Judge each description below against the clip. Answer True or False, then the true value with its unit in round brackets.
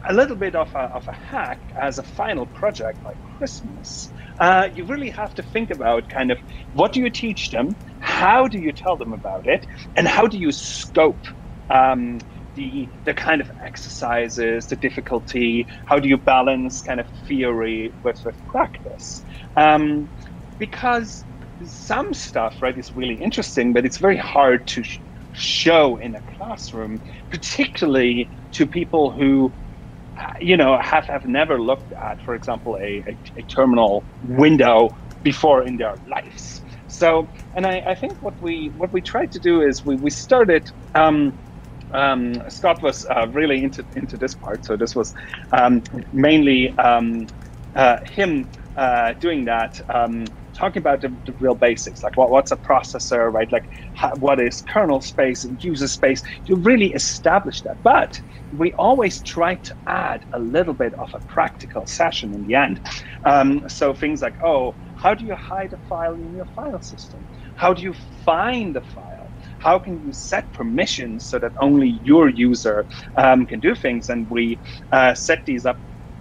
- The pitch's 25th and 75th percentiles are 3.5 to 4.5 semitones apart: False (5.5 semitones)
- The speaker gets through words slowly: False (170 wpm)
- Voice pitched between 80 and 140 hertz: True (135 Hz)